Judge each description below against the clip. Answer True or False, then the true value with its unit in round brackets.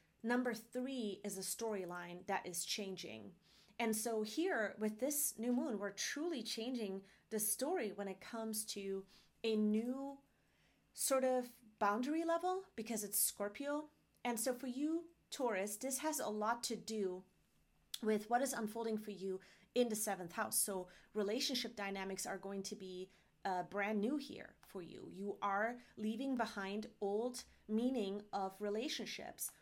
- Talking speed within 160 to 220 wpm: False (150 wpm)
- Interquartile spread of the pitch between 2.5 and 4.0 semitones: True (3.7 semitones)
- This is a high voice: True (215 Hz)